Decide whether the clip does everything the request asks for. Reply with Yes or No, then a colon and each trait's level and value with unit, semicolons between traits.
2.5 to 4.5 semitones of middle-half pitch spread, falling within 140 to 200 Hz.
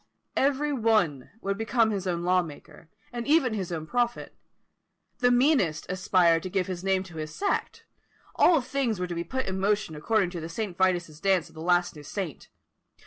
No: average, 4.9 semitones; high, 190 Hz